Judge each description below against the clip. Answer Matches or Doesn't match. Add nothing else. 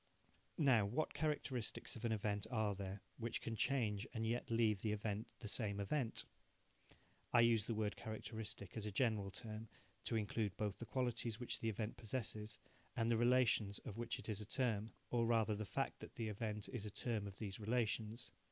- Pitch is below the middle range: Matches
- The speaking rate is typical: Matches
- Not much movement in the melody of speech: Matches